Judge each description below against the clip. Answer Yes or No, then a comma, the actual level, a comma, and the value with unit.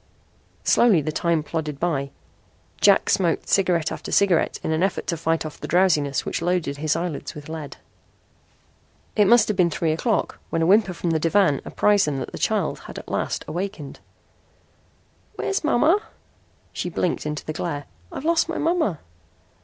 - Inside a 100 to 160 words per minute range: No, average, 170 wpm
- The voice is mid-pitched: Yes, medium, 170 Hz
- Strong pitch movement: No, average, 4.3 semitones